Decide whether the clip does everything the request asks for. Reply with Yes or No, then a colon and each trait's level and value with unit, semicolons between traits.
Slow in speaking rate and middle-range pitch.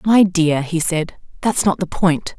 No: average, 200 wpm; medium, 175 Hz